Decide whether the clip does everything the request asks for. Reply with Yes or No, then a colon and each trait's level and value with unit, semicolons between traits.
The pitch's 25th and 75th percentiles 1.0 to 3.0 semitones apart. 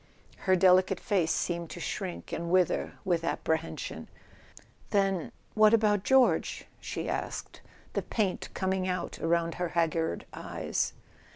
Yes: narrow, 2.4 semitones